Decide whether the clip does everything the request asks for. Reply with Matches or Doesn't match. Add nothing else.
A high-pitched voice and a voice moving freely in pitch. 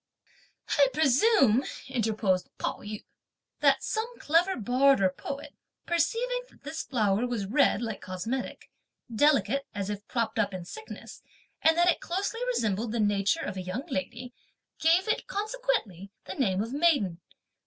Matches